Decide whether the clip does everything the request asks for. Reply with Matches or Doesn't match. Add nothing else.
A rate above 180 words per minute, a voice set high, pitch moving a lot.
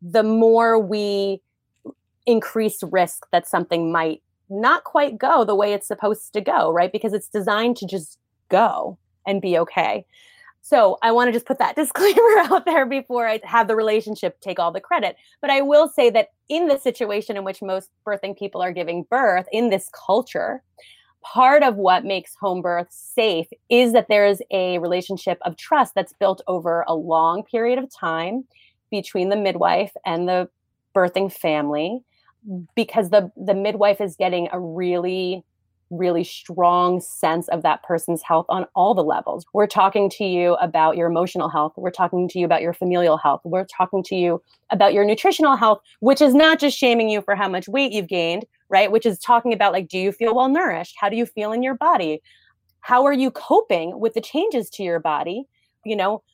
Doesn't match